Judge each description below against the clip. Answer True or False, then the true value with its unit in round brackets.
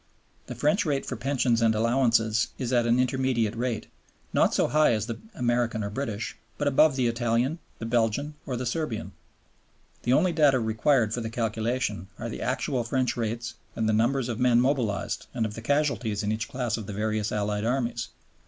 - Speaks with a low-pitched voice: True (120 Hz)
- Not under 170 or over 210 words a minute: True (190 wpm)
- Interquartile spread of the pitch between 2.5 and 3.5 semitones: True (2.8 semitones)